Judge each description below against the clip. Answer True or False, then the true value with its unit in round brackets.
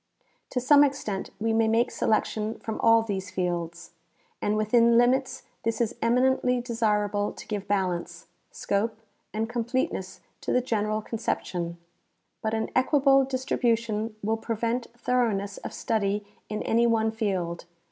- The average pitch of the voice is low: False (225 Hz)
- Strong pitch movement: False (2.6 semitones)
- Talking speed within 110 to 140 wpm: True (135 wpm)